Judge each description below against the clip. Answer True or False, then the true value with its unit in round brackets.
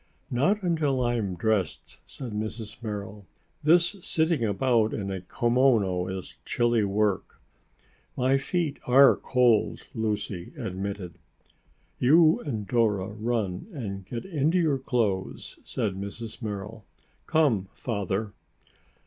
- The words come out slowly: True (115 wpm)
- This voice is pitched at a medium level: False (110 Hz)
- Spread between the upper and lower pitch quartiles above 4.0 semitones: True (4.9 semitones)